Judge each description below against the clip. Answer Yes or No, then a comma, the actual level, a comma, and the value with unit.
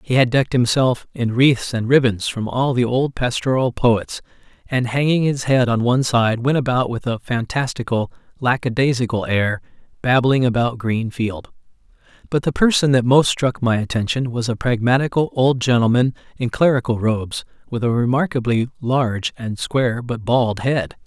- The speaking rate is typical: Yes, average, 160 wpm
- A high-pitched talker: No, low, 125 Hz